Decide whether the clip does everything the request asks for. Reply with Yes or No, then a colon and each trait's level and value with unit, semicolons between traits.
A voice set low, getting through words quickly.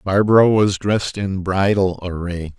No: very low, 95 Hz; average, 140 wpm